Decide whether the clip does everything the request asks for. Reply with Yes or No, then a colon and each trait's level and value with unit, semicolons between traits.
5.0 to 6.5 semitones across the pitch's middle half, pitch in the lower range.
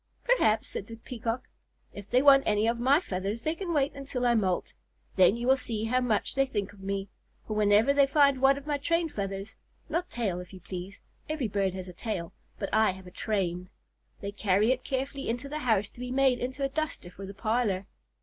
No: wide, 5.5 semitones; high, 230 Hz